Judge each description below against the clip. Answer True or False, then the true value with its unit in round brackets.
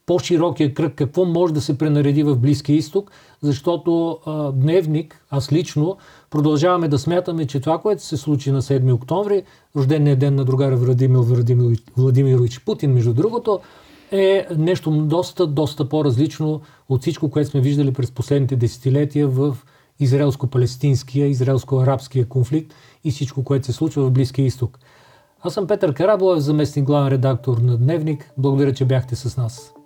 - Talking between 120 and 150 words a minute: True (145 wpm)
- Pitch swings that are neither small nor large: True (3.1 semitones)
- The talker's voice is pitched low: False (145 Hz)